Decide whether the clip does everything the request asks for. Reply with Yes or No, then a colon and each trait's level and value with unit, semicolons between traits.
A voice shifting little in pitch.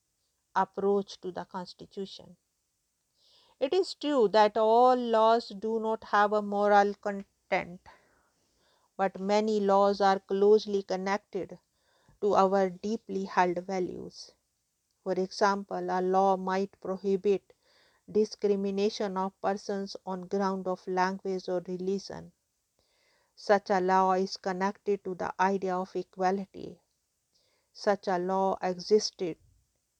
Yes: narrow, 2.1 semitones